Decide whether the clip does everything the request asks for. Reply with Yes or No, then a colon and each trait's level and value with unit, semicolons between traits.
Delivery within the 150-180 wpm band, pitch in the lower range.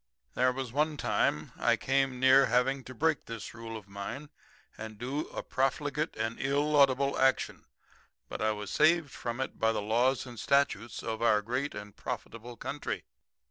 Yes: average, 170 wpm; low, 130 Hz